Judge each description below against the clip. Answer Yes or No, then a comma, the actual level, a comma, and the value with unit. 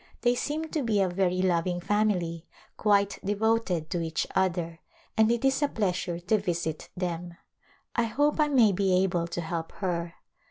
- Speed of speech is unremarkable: Yes, average, 170 wpm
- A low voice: No, high, 190 Hz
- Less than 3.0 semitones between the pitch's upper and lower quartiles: No, average, 4.4 semitones